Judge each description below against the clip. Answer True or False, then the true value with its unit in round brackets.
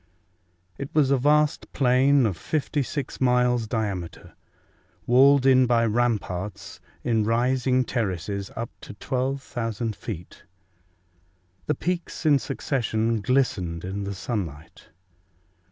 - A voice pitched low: True (120 Hz)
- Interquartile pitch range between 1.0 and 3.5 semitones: False (4.3 semitones)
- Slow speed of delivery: True (105 wpm)